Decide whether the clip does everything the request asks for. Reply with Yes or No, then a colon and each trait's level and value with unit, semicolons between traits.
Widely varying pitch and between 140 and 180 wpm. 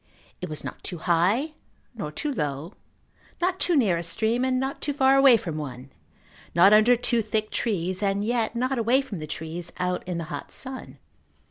No: wide, 7.2 semitones; average, 195 wpm